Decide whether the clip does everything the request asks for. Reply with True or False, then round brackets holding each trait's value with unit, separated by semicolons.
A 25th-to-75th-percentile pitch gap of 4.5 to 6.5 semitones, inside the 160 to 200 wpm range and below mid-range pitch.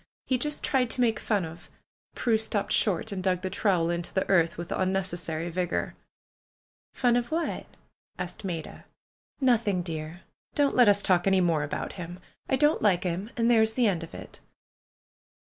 False (4.8 semitones; 180 wpm; 190 Hz)